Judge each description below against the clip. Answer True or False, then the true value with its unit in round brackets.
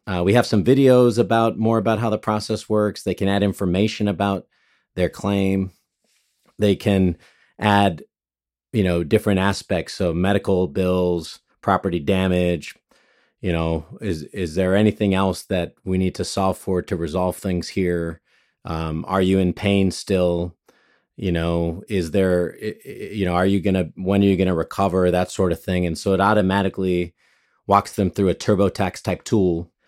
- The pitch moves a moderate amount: False (2.2 semitones)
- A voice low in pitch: True (95 Hz)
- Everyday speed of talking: True (165 wpm)